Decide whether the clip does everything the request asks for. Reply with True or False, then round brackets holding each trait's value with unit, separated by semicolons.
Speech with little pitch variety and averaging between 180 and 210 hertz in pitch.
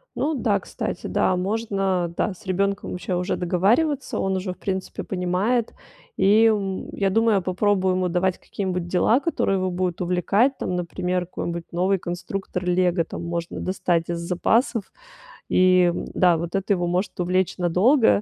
True (1.9 semitones; 185 Hz)